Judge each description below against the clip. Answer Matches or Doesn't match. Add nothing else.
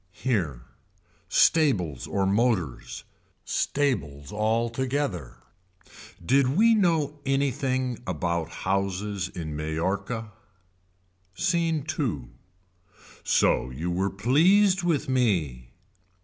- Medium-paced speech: Doesn't match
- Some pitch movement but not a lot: Doesn't match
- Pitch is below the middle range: Matches